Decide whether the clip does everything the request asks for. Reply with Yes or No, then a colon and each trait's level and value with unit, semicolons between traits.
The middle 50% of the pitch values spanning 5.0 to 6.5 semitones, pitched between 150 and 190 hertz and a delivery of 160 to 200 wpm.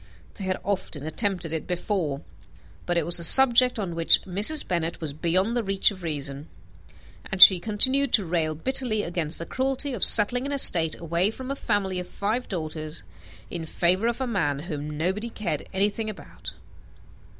Yes: average, 5.3 semitones; medium, 185 Hz; average, 175 wpm